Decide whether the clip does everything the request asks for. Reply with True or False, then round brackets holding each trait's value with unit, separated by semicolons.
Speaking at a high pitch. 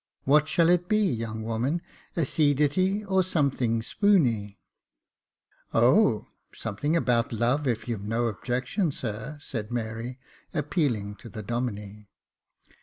False (125 Hz)